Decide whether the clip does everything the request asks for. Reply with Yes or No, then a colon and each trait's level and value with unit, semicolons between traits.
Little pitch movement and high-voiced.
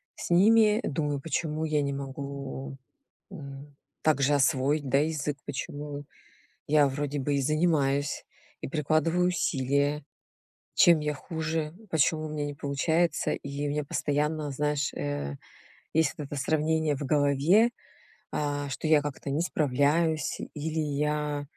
No: narrow, 1.9 semitones; medium, 145 Hz